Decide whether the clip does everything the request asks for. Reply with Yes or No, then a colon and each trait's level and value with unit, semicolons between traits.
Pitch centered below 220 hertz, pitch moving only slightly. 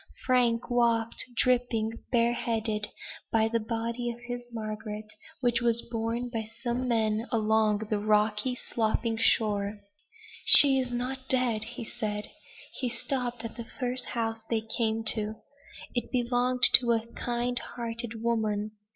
No: high, 230 Hz; narrow, 1.8 semitones